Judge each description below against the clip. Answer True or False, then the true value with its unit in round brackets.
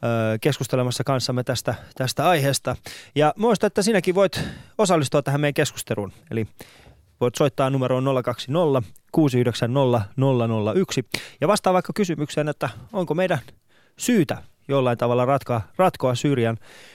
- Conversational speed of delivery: True (120 wpm)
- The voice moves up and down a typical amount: True (4.4 semitones)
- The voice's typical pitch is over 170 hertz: False (135 Hz)